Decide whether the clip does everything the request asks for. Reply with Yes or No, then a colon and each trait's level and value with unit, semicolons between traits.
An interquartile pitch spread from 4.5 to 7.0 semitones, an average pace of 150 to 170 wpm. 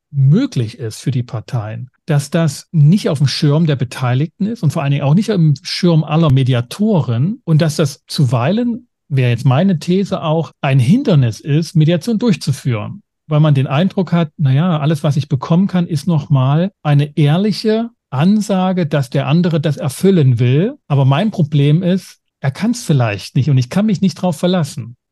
No: average, 4.8 semitones; average, 185 wpm